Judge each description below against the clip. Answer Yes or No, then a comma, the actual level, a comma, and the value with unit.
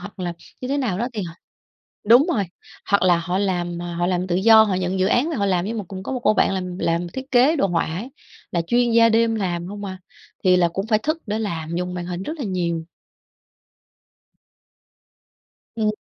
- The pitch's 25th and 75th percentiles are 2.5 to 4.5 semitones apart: Yes, average, 4.2 semitones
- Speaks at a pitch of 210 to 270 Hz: No, high, 195 Hz